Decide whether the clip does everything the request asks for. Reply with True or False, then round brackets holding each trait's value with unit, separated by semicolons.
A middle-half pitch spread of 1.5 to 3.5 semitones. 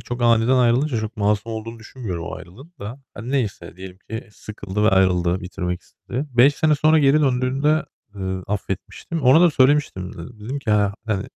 False (5.2 semitones)